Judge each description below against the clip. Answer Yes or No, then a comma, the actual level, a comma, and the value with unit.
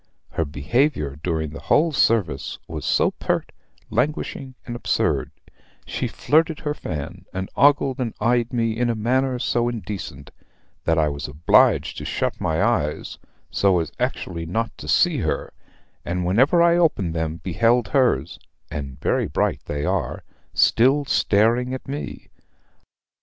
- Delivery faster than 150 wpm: No, average, 145 wpm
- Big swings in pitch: Yes, wide, 7.8 semitones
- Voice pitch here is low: Yes, low, 110 Hz